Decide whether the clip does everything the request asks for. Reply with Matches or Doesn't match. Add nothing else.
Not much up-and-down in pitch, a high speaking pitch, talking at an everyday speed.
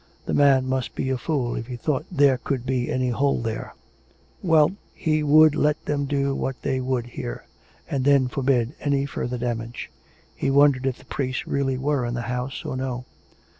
Doesn't match